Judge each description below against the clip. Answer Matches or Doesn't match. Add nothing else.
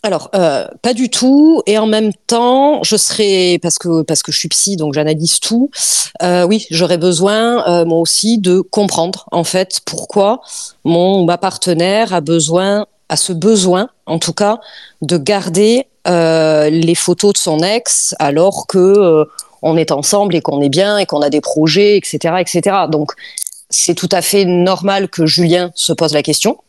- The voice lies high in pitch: Doesn't match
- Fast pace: Doesn't match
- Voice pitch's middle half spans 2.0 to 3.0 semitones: Doesn't match